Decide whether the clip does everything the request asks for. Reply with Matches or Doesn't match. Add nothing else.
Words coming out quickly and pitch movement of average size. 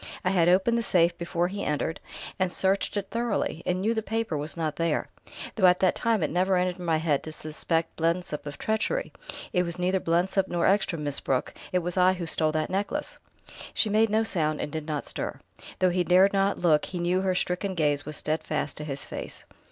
Matches